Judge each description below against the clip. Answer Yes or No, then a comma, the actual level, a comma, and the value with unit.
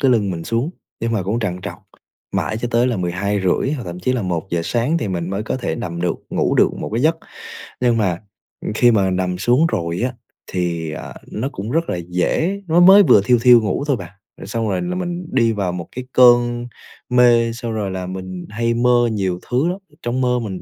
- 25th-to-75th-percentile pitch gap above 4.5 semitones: Yes, average, 5.0 semitones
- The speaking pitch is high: No, low, 115 Hz